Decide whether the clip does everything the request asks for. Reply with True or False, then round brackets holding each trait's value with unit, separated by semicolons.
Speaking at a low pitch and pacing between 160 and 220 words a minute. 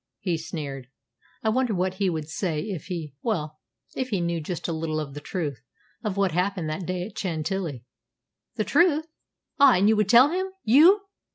False (185 Hz; 190 wpm)